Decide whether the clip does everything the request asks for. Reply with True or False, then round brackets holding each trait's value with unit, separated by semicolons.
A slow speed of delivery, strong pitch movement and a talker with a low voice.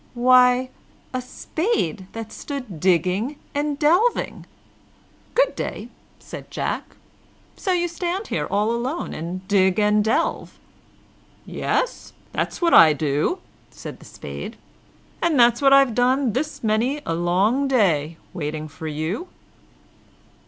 False (130 wpm; 7.7 semitones; 240 Hz)